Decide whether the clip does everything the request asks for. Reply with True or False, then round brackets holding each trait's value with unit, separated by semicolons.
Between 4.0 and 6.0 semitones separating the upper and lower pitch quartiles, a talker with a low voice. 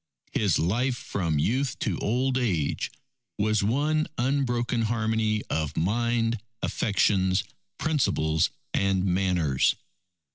True (4.6 semitones; 110 Hz)